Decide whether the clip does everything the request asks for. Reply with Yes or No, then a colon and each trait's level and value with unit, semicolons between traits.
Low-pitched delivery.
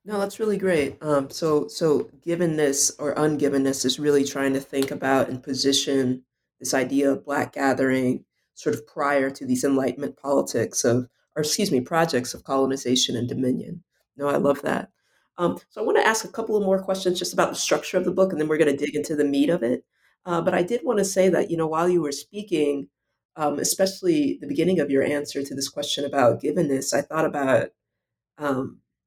No: medium, 145 Hz